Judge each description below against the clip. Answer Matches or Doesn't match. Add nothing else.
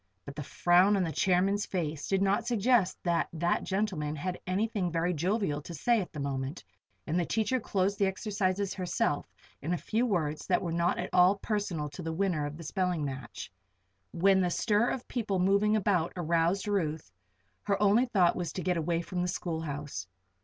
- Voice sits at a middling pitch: Matches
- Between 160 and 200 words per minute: Matches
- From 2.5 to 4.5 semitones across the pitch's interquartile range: Matches